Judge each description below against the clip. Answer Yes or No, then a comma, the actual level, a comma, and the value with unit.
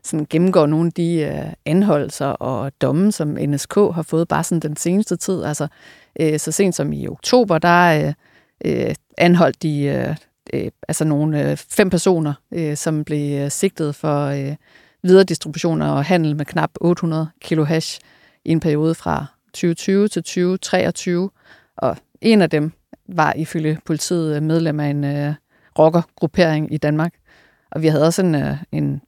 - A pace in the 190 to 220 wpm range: No, average, 165 wpm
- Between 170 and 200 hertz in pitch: No, medium, 160 Hz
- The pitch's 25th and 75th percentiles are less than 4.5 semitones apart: Yes, average, 2.8 semitones